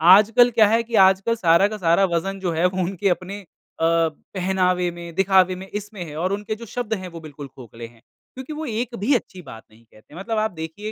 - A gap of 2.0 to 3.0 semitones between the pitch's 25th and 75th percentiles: No, average, 4.1 semitones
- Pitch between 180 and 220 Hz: Yes, high, 190 Hz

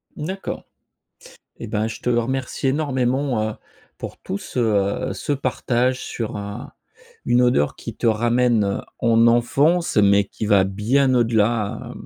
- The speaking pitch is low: Yes, low, 120 Hz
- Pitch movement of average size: Yes, average, 3.4 semitones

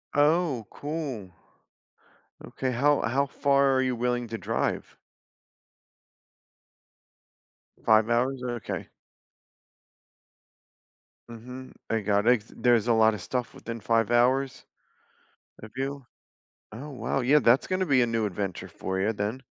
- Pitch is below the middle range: Yes, low, 120 Hz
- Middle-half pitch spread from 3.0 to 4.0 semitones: Yes, average, 3.3 semitones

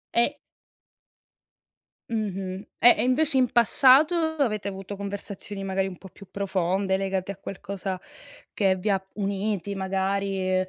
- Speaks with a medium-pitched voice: No, high, 195 Hz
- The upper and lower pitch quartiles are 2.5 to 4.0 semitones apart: No, narrow, 1.9 semitones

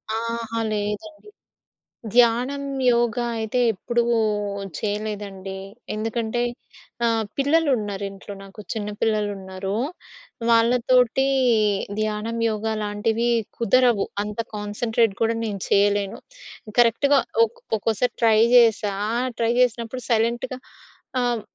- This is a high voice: Yes, high, 225 Hz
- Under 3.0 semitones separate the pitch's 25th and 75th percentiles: Yes, narrow, 2.4 semitones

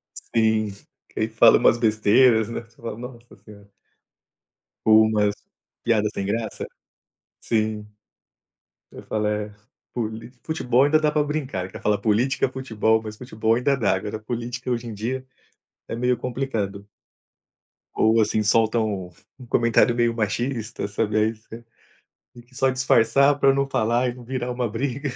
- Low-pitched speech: Yes, low, 115 Hz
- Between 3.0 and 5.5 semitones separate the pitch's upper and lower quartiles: No, narrow, 2.6 semitones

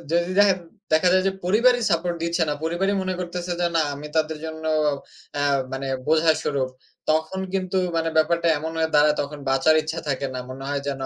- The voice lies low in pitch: No, medium, 160 Hz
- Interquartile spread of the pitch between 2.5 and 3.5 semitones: Yes, average, 3.2 semitones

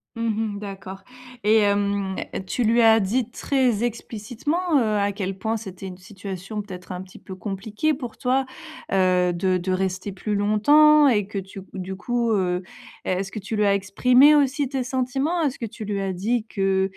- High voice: Yes, high, 210 Hz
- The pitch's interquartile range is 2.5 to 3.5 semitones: No, average, 4.1 semitones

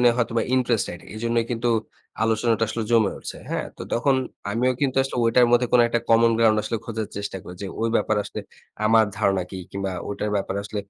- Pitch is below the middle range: Yes, low, 115 Hz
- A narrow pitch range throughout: Yes, narrow, 2.2 semitones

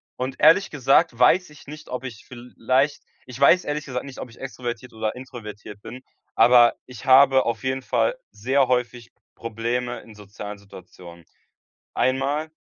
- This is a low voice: Yes, low, 125 Hz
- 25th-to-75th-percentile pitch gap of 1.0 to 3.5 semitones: Yes, average, 2.7 semitones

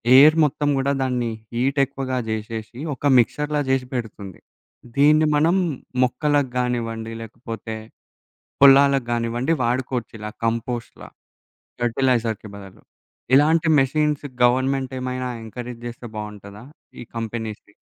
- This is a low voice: Yes, low, 125 Hz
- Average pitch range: Yes, average, 3.2 semitones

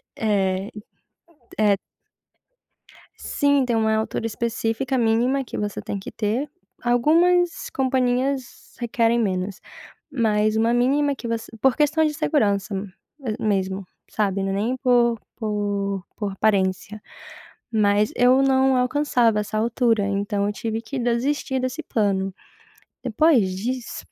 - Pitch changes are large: No, average, 3.9 semitones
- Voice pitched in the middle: No, high, 225 Hz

